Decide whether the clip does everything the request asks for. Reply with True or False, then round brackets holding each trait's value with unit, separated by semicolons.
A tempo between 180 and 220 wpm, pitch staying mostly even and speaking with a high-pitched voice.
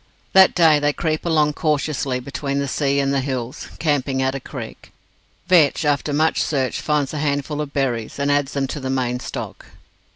False (190 wpm; 2.1 semitones; 140 Hz)